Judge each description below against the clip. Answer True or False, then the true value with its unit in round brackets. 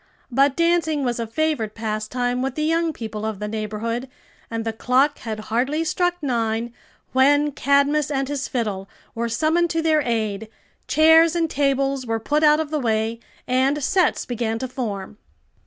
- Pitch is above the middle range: True (260 Hz)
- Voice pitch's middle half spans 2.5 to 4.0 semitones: False (5.0 semitones)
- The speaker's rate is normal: True (170 wpm)